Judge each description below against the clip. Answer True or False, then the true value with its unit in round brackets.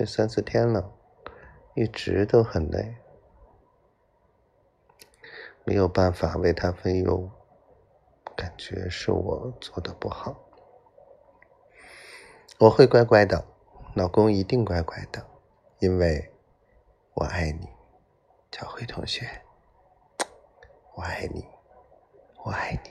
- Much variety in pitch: False (4.2 semitones)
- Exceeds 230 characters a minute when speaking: False (135 characters per minute)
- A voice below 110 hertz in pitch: True (100 Hz)